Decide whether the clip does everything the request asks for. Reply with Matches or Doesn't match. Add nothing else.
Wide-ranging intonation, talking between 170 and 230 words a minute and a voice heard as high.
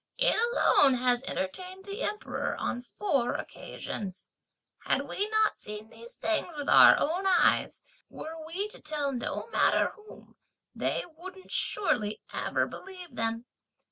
Doesn't match